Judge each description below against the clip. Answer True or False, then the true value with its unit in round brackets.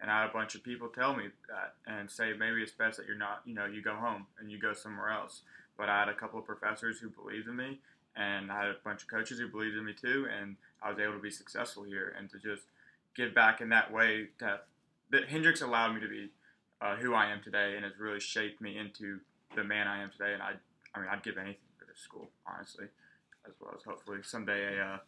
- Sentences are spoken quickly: True (260 wpm)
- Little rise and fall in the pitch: True (1.5 semitones)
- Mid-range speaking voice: False (105 Hz)